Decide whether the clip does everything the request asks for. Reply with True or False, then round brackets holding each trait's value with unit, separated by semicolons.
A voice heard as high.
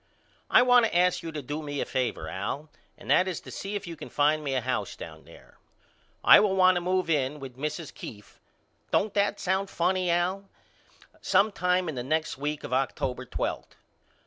False (165 Hz)